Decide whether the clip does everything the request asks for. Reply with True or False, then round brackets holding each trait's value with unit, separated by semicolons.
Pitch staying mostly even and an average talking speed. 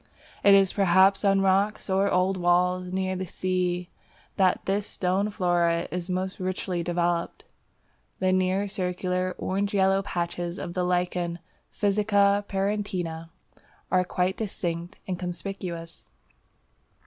False (1.7 semitones; 125 wpm)